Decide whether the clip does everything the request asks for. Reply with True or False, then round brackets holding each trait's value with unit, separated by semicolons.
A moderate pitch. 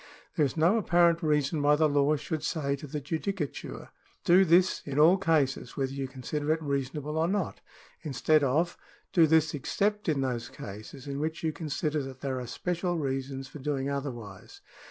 True (150 Hz)